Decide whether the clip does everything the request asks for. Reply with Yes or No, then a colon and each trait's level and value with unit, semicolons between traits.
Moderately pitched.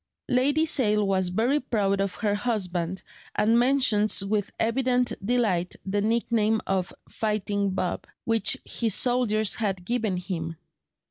No: high, 215 Hz